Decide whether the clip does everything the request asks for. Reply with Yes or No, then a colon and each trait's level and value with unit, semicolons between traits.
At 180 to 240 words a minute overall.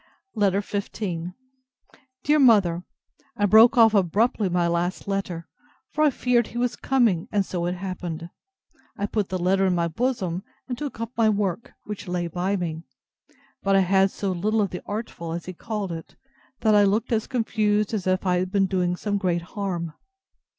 Yes: average, 185 wpm